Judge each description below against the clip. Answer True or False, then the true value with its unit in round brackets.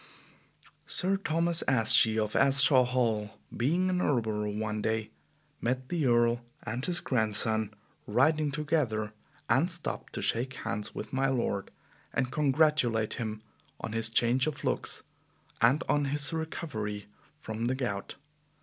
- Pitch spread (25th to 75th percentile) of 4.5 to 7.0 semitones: True (5.1 semitones)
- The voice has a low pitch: True (125 Hz)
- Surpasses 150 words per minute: False (135 wpm)